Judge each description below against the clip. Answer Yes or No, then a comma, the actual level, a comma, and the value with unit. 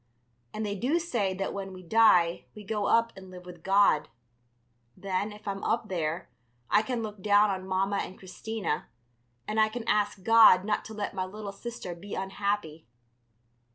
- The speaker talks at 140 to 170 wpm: No, average, 180 wpm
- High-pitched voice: Yes, high, 200 Hz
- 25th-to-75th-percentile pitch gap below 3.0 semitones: Yes, narrow, 2.5 semitones